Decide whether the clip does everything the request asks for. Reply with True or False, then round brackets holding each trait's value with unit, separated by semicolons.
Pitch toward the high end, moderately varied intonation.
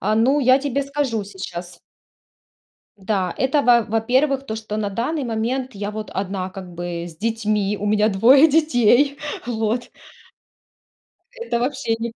True (225 Hz; 4.5 semitones)